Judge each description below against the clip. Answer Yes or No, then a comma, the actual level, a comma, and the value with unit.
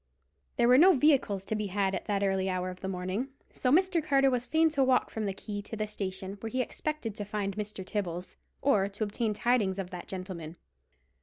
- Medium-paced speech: No, fast, 220 wpm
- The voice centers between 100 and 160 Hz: No, high, 210 Hz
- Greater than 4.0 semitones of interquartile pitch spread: Yes, average, 4.7 semitones